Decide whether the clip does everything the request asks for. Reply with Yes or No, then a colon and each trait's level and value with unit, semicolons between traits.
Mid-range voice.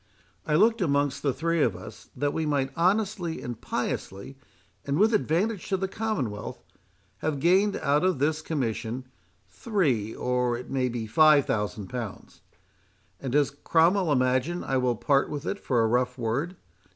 Yes: medium, 145 Hz